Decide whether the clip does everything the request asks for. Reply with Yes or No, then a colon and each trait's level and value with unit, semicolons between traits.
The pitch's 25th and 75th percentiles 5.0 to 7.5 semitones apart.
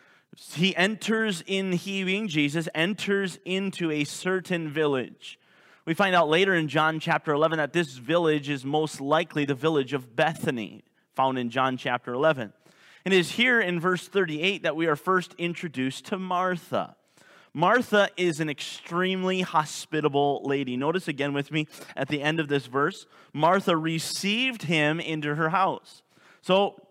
No: average, 3.9 semitones